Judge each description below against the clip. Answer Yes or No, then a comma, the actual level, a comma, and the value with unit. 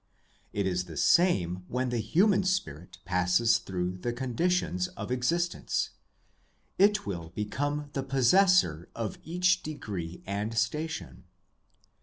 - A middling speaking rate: No, slow, 120 wpm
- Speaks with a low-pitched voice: Yes, low, 120 Hz